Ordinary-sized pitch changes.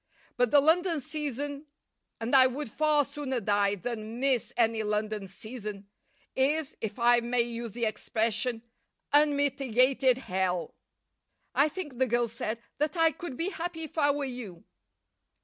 Yes: average, 4.6 semitones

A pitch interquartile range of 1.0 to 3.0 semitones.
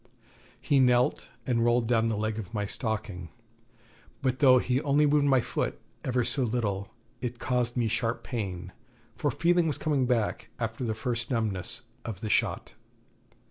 Yes: average, 2.7 semitones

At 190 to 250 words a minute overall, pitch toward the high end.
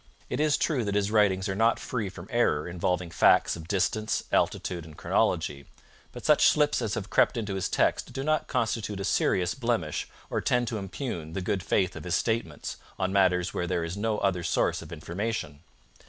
No: average, 200 wpm; low, 100 Hz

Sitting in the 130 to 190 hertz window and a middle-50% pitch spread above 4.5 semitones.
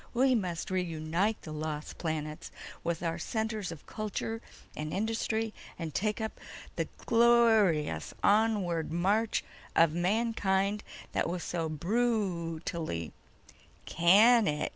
Yes: medium, 185 Hz; average, 5.1 semitones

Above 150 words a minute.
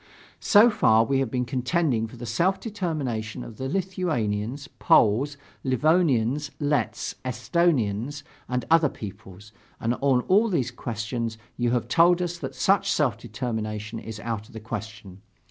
No: average, 145 wpm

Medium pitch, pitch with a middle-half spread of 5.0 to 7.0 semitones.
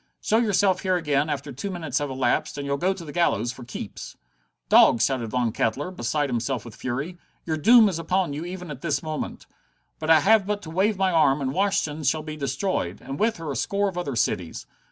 Yes: medium, 155 Hz; wide, 5.4 semitones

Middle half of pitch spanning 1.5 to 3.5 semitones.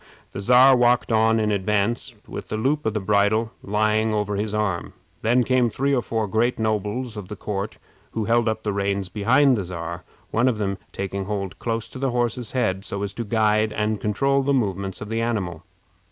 Yes: average, 2.8 semitones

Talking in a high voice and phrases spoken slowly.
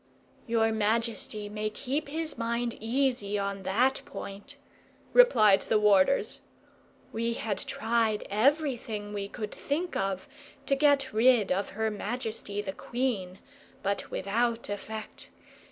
Yes: high, 220 Hz; slow, 120 wpm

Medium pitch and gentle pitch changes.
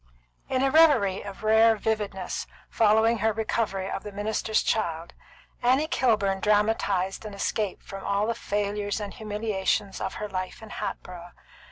No: high, 210 Hz; narrow, 2.2 semitones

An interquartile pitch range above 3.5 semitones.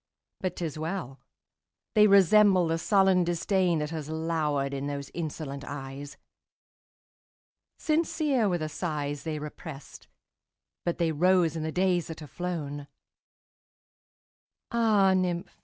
Yes: average, 4.0 semitones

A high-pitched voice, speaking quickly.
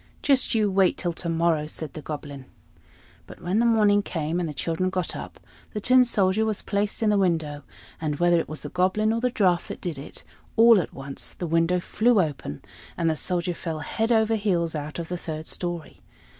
No: medium, 175 Hz; fast, 210 wpm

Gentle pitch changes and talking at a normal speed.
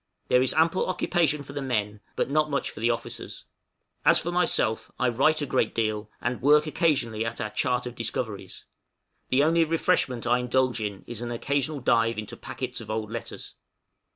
No: average, 4.5 semitones; average, 185 wpm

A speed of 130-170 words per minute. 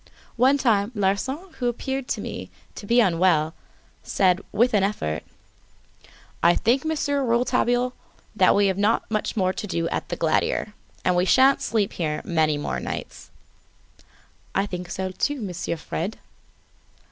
Yes: average, 155 wpm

